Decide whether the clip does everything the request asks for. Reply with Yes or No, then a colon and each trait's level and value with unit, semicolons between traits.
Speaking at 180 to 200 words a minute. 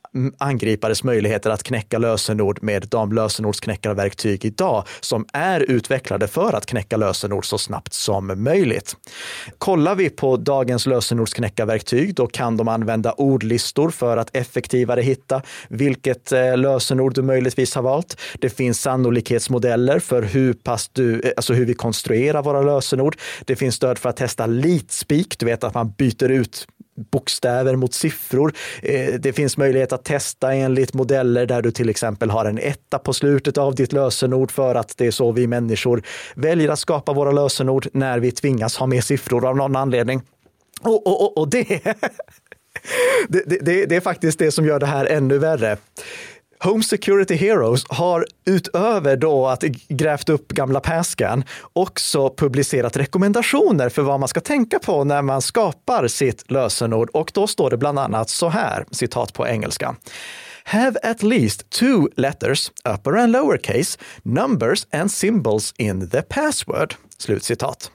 No: average, 155 wpm